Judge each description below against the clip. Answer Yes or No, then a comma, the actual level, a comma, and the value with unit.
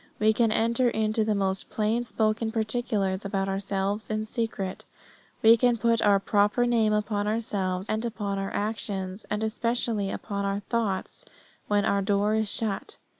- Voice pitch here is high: Yes, high, 215 Hz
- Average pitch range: No, narrow, 2.1 semitones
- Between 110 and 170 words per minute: Yes, average, 160 wpm